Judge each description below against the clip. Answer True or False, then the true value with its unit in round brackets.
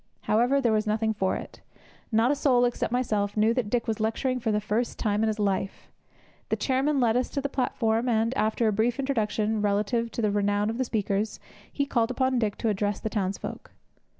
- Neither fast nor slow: False (210 wpm)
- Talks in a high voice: True (225 Hz)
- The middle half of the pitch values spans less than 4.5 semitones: True (2.7 semitones)